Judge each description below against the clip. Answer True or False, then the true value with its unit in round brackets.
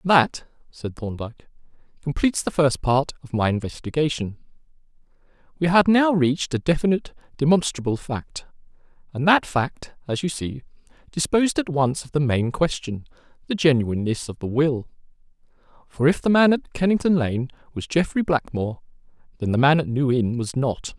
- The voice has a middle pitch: True (145 Hz)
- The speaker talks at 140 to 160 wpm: True (150 wpm)